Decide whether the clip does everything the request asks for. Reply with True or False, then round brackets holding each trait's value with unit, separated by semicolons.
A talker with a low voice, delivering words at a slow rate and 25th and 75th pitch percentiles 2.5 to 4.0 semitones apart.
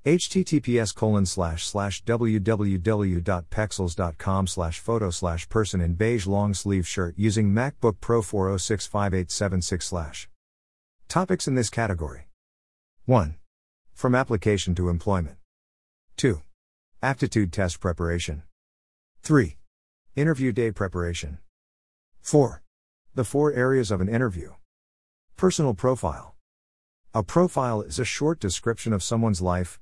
False (95 Hz; 95 wpm; 5.6 semitones)